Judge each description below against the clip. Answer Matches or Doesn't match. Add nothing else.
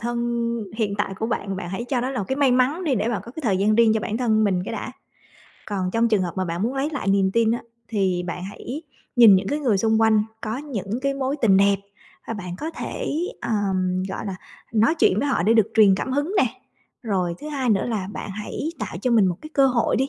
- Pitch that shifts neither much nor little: Matches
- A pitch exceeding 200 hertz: Matches